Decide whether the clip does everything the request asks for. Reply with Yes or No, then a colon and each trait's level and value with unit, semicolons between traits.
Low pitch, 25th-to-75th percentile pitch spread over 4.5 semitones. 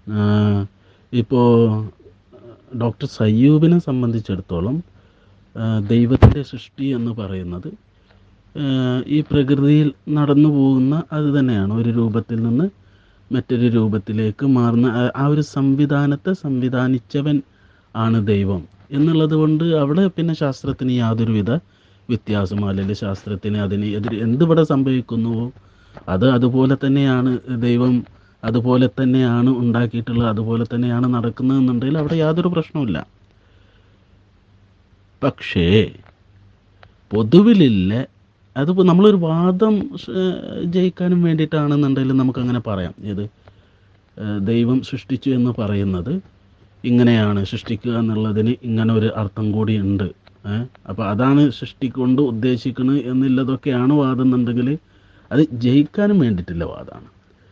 Yes: low, 120 Hz; average, 5.0 semitones